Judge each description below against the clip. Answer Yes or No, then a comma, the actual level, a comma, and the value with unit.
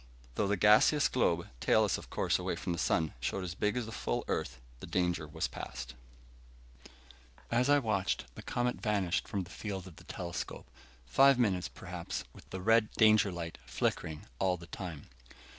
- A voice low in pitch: Yes, very low, 95 Hz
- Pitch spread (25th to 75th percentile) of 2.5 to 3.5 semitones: No, average, 4.2 semitones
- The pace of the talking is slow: No, average, 175 wpm